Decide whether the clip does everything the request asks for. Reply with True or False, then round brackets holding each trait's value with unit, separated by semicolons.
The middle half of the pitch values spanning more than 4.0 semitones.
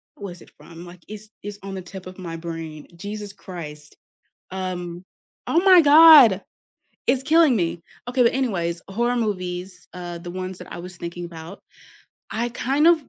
True (5.3 semitones)